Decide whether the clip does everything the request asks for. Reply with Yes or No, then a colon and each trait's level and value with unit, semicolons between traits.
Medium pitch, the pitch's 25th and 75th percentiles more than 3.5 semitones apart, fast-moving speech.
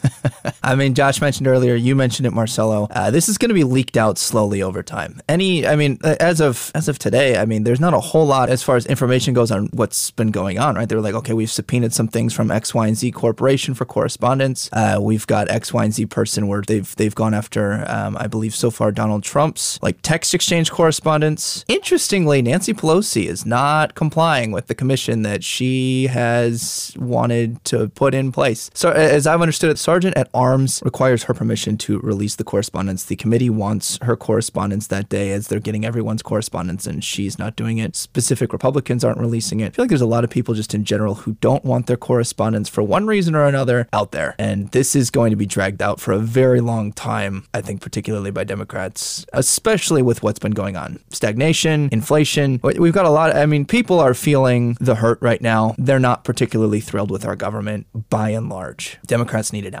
No: low, 120 Hz; average, 4.2 semitones; fast, 220 wpm